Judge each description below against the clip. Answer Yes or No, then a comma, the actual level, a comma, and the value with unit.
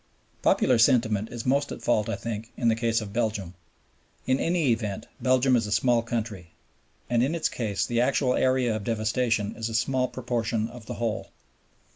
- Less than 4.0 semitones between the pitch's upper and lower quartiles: Yes, narrow, 2.5 semitones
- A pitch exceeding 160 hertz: No, low, 115 Hz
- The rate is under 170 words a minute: No, average, 185 wpm